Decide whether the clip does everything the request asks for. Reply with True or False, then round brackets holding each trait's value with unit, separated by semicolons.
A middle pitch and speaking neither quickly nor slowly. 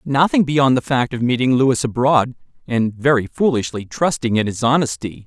False (130 Hz; 170 wpm)